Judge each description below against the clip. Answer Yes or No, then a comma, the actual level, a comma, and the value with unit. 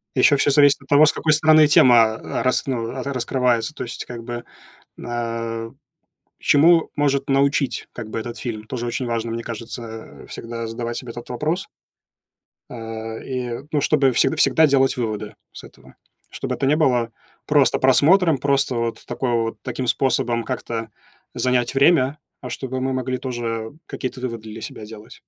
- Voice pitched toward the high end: No, low, 125 Hz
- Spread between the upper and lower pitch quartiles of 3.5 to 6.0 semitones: No, average, 3.0 semitones